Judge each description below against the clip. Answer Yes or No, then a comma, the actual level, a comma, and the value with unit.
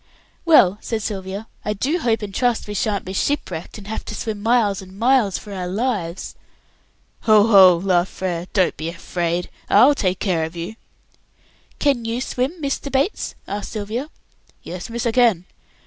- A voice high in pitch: Yes, high, 205 Hz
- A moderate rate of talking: Yes, average, 170 wpm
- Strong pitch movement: No, average, 4.3 semitones